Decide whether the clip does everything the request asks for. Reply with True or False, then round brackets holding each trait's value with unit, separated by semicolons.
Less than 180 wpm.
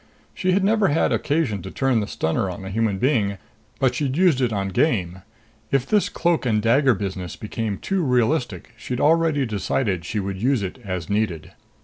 False (190 wpm)